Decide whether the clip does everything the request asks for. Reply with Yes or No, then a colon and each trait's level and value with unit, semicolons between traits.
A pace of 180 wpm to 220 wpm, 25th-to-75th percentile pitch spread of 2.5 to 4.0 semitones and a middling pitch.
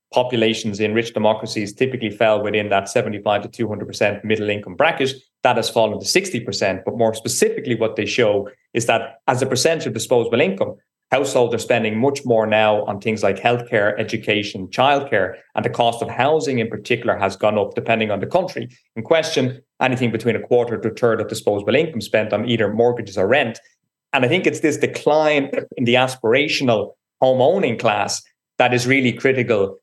No: average, 185 wpm; average, 3.0 semitones; low, 115 Hz